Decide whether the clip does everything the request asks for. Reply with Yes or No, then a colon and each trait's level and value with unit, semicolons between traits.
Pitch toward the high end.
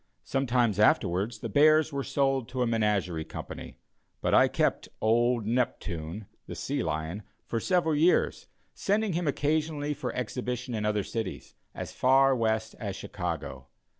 No: low, 120 Hz